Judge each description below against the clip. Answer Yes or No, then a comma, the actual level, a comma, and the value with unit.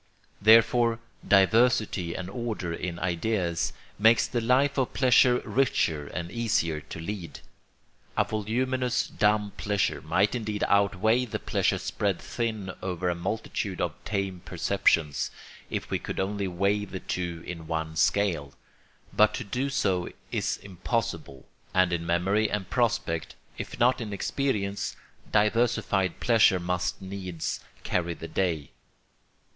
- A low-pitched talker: Yes, low, 100 Hz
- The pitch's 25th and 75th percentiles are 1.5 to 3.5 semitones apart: No, average, 4.4 semitones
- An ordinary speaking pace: No, slow, 130 wpm